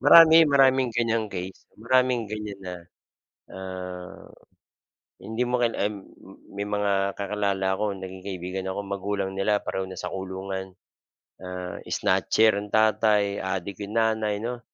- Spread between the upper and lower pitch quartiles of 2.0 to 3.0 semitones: Yes, narrow, 2.6 semitones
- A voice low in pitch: Yes, low, 100 Hz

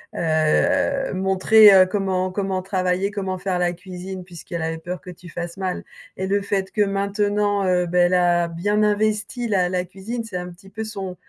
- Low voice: No, high, 190 Hz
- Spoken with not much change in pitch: Yes, narrow, 2.2 semitones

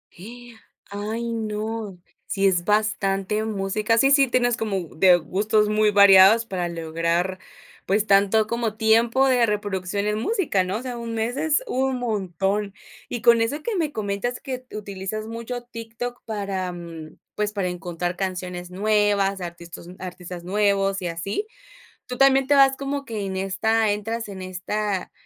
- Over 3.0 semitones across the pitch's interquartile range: Yes, average, 3.5 semitones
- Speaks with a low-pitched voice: No, high, 210 Hz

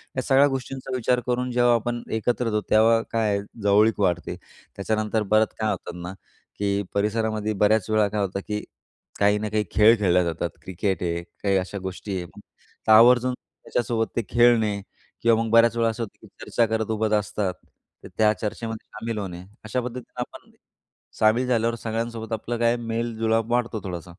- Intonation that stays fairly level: Yes, narrow, 2.3 semitones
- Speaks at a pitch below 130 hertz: Yes, low, 110 Hz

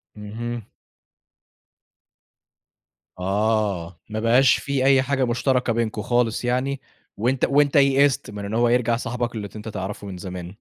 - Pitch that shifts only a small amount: No, average, 3.7 semitones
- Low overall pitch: Yes, low, 115 Hz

